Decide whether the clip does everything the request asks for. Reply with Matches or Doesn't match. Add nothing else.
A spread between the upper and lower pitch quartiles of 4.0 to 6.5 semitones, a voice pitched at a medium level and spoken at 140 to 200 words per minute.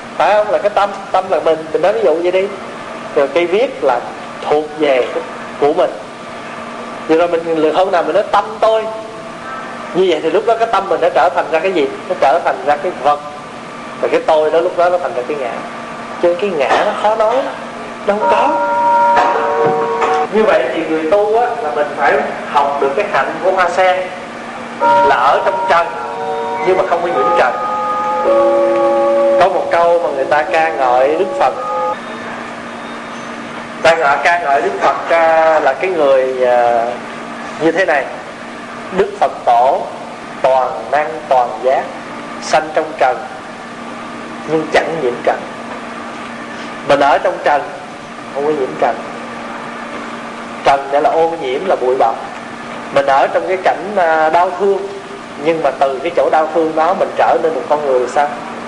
Matches